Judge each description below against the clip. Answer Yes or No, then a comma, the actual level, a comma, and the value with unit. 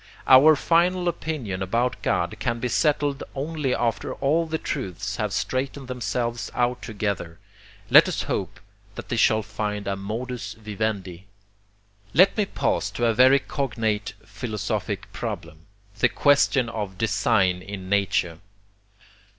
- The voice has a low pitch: Yes, low, 115 Hz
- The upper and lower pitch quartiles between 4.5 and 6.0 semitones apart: Yes, average, 5.1 semitones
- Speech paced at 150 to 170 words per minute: No, slow, 135 wpm